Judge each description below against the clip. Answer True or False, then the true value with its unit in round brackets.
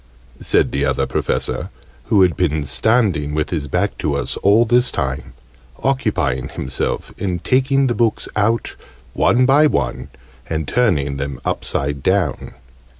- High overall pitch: False (90 Hz)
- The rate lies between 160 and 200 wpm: False (145 wpm)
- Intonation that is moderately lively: False (9.0 semitones)